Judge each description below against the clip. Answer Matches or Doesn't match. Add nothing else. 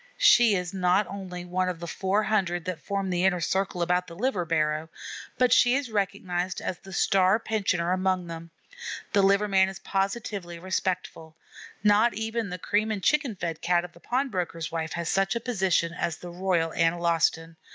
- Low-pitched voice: Doesn't match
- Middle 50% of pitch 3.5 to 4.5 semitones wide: Doesn't match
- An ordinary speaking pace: Matches